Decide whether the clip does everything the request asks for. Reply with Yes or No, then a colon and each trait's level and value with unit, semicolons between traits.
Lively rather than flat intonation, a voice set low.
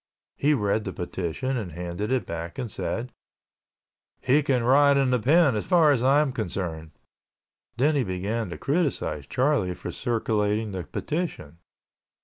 Yes: wide, 7.0 semitones; low, 115 Hz